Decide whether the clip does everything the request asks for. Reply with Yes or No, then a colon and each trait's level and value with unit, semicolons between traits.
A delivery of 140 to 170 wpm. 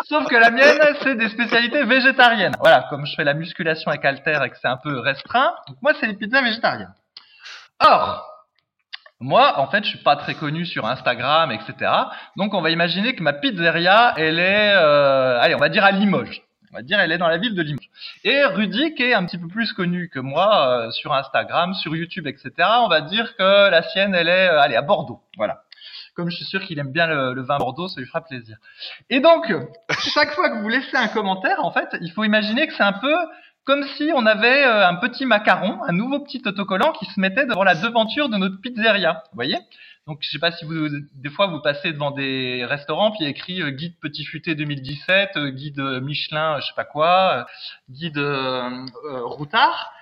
No: fast, 220 wpm